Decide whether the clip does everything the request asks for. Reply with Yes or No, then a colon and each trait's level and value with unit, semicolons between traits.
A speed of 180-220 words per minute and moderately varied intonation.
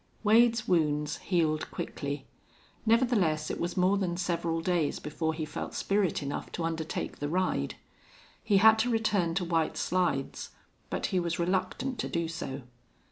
No: average, 155 wpm; average, 3.7 semitones